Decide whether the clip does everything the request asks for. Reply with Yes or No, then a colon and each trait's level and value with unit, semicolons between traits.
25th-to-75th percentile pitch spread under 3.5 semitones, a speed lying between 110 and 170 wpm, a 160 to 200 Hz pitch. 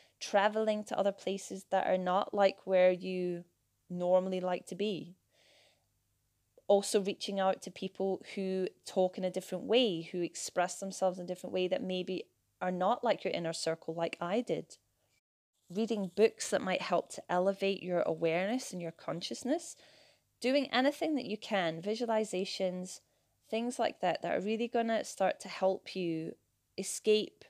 Yes: average, 2.8 semitones; average, 160 wpm; high, 190 Hz